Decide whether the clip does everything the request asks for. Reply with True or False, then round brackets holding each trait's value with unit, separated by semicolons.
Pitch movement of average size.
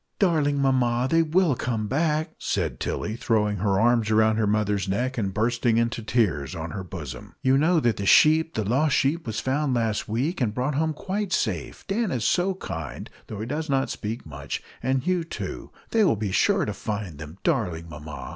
False (6.6 semitones)